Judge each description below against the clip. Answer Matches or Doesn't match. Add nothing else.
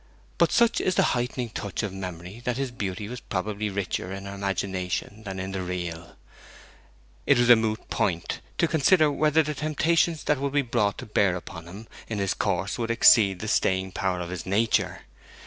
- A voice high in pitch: Doesn't match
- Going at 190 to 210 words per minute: Matches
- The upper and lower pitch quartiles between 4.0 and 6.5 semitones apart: Matches